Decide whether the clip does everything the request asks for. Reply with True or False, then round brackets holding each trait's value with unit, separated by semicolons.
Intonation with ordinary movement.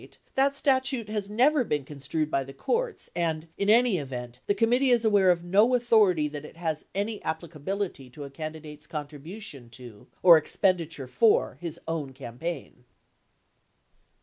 False (6.6 semitones)